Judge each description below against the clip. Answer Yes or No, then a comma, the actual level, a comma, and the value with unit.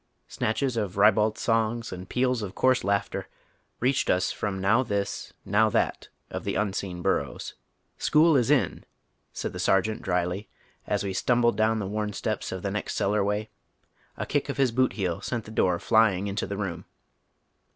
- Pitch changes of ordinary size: Yes, average, 3.0 semitones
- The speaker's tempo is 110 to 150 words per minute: No, average, 180 wpm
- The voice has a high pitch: No, low, 105 Hz